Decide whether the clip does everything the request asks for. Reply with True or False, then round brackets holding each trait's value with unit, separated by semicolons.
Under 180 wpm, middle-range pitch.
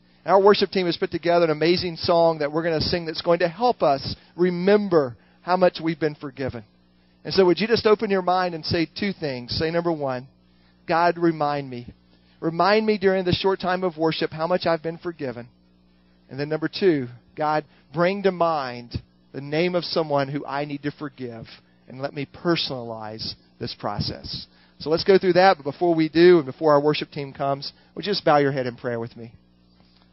False (205 wpm; 155 Hz)